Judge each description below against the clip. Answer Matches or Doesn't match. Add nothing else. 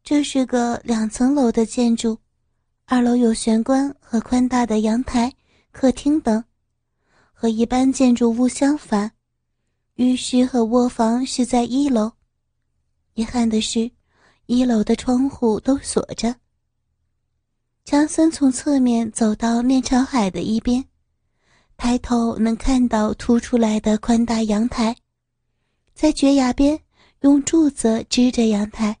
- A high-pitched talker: Matches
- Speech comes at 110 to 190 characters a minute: Matches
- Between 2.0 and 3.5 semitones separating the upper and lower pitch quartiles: Matches